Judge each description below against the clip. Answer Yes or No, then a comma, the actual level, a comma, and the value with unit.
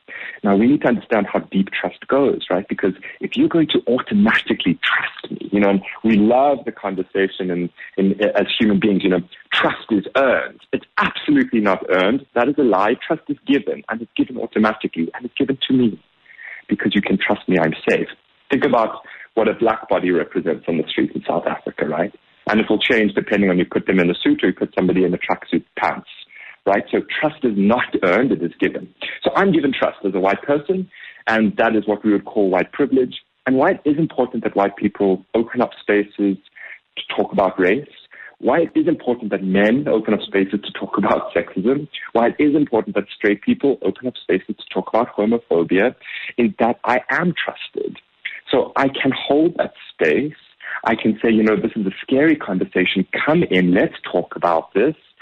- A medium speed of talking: No, fast, 210 wpm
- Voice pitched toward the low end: Yes, low, 115 Hz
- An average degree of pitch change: No, wide, 6.2 semitones